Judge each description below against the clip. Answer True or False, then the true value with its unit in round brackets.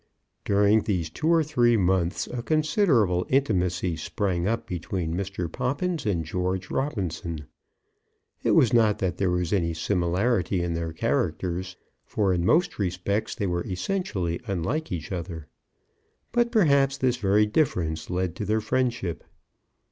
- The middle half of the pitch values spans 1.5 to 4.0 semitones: False (5.6 semitones)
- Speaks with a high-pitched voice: False (95 Hz)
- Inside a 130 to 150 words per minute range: True (140 wpm)